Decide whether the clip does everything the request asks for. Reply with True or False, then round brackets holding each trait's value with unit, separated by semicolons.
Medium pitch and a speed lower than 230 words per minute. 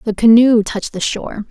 False (220 Hz; 200 wpm)